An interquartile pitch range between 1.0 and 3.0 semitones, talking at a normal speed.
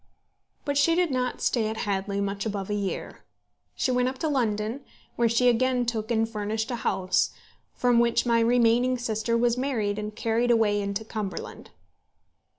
Yes: average, 2.7 semitones; average, 170 wpm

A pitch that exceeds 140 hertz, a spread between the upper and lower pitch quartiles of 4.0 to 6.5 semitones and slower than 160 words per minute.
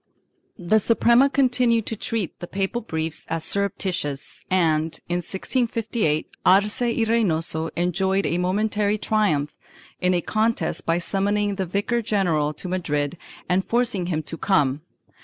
Yes: high, 190 Hz; average, 4.8 semitones; average, 145 wpm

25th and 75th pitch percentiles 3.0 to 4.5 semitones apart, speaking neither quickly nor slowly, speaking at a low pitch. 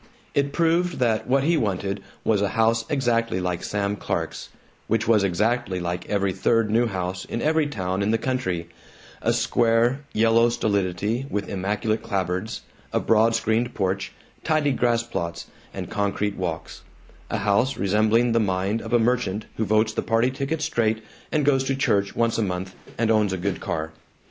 Yes: average, 3.5 semitones; average, 175 wpm; low, 110 Hz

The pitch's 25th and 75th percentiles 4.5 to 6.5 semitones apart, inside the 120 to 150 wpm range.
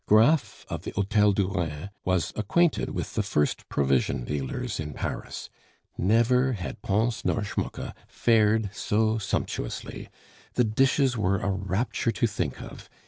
No: average, 3.8 semitones; average, 140 wpm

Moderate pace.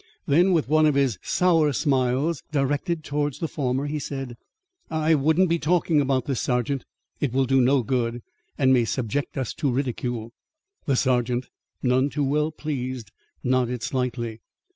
Yes: average, 160 wpm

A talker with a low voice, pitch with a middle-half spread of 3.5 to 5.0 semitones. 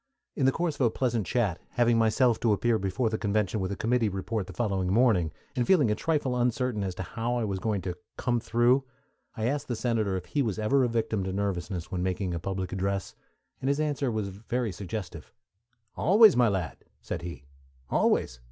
Yes: low, 110 Hz; average, 4.3 semitones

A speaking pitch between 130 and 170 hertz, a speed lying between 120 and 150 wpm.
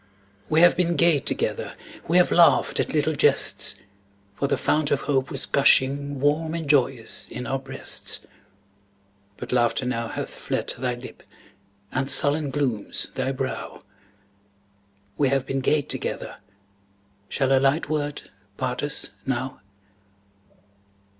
Yes: medium, 140 Hz; slow, 135 wpm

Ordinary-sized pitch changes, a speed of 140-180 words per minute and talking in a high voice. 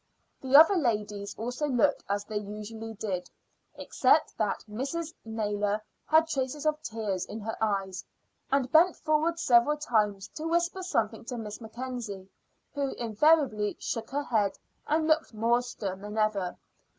No: wide, 6.0 semitones; average, 150 wpm; high, 230 Hz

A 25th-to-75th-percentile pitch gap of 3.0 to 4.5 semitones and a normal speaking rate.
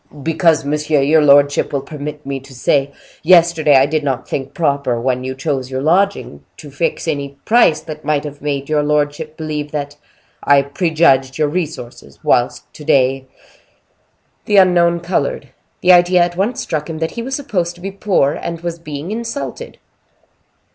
Yes: average, 3.4 semitones; average, 170 wpm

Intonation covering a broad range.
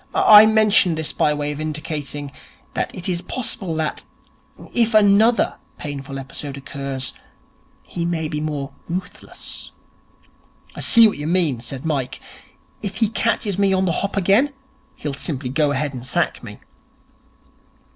Yes: wide, 5.8 semitones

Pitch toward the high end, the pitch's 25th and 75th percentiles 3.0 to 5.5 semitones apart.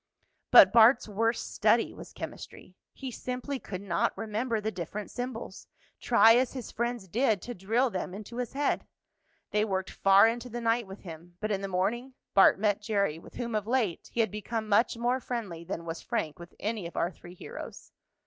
Yes: high, 215 Hz; average, 3.8 semitones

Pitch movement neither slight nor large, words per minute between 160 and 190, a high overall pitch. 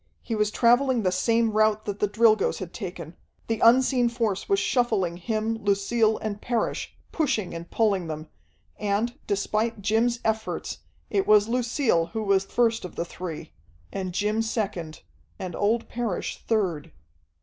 No: average, 3.2 semitones; average, 150 wpm; high, 215 Hz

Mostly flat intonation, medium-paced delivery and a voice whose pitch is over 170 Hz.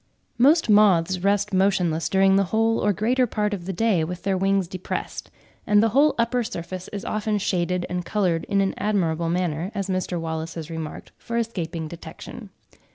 No: average, 3.5 semitones; average, 180 wpm; high, 190 Hz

